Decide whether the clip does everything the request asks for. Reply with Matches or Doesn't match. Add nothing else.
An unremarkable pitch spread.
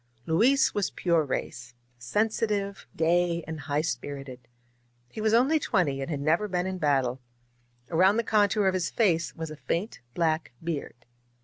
Doesn't match